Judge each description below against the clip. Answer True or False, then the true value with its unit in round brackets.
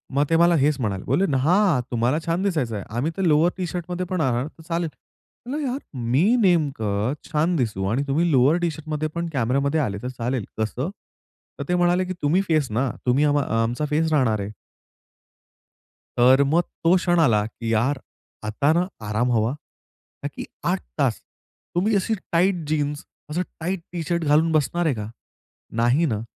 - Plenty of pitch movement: True (5.8 semitones)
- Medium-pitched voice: True (150 Hz)